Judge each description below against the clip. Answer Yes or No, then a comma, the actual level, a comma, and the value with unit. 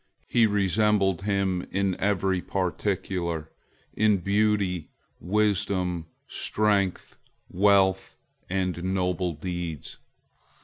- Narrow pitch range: Yes, narrow, 2.1 semitones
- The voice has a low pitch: Yes, very low, 95 Hz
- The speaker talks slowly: Yes, slow, 75 wpm